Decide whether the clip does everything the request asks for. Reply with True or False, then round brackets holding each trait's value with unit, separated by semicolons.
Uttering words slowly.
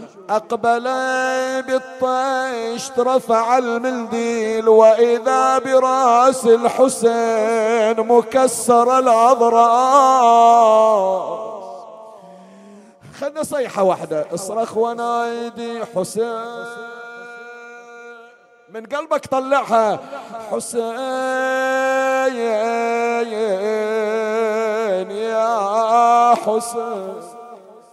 True (45 wpm)